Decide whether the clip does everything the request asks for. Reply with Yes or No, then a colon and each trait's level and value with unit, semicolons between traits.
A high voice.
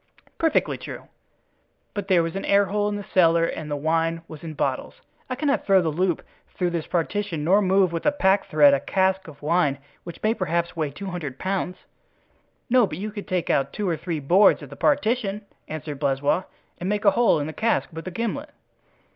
No: medium, 180 Hz